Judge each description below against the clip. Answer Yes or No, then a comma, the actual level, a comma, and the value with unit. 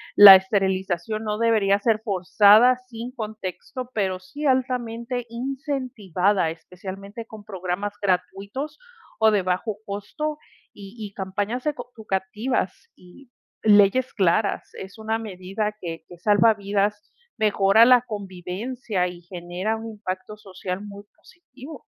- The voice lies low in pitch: No, high, 210 Hz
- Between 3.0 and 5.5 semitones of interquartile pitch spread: Yes, average, 3.3 semitones